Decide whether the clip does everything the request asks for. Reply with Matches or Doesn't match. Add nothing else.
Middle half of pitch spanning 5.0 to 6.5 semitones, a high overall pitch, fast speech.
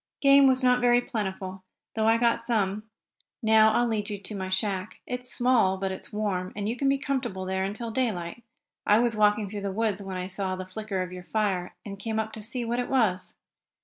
Doesn't match